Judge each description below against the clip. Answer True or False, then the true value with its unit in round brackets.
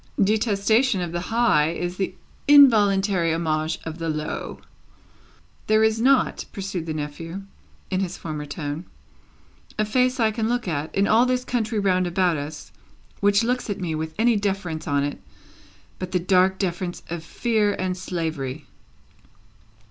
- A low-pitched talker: False (185 Hz)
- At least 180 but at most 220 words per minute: False (155 wpm)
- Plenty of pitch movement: False (4.9 semitones)